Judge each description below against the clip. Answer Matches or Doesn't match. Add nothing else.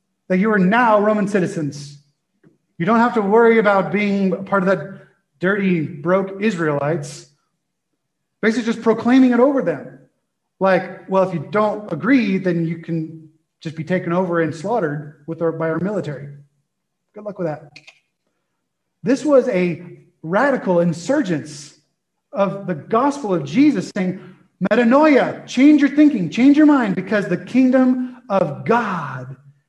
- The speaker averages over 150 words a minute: Doesn't match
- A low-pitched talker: Doesn't match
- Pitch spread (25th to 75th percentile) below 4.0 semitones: Doesn't match